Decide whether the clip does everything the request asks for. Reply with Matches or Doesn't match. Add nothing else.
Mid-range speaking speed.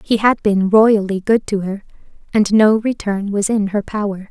Matches